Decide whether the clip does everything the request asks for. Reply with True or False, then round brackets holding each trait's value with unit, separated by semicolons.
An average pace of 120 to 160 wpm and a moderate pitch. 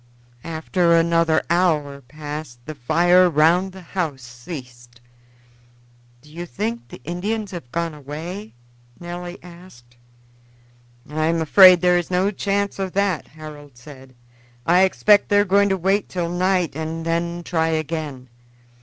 True (140 wpm; 170 Hz)